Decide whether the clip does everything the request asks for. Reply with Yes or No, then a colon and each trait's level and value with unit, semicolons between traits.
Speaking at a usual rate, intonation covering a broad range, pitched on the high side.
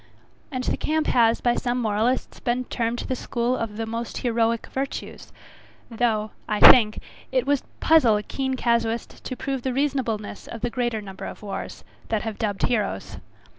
No: average, 170 wpm; narrow, 2.4 semitones; high, 235 Hz